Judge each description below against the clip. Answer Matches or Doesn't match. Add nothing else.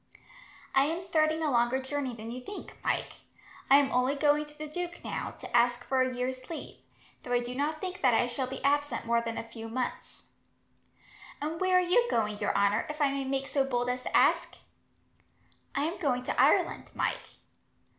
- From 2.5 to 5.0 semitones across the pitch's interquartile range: Matches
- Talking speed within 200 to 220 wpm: Matches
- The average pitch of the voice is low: Doesn't match